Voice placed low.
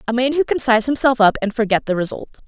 No: high, 235 Hz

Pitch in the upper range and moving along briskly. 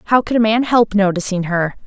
Yes: high, 210 Hz; fast, 225 wpm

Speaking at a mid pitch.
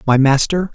Yes: medium, 145 Hz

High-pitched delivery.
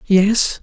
Yes: high, 200 Hz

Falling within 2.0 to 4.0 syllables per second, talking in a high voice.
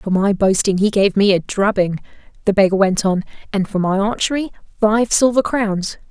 No: 5.1 syllables/s; high, 200 Hz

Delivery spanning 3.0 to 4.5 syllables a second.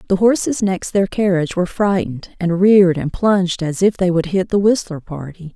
No: 5.5 syllables/s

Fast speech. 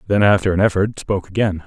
Yes: fast, 215 wpm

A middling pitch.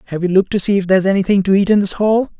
No: high, 195 Hz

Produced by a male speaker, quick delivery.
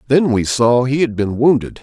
Yes: male; fast, 230 wpm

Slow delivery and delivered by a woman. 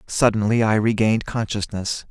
No: slow, 115 wpm; male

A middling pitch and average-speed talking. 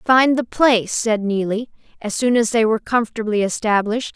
No: high, 225 Hz; average, 175 wpm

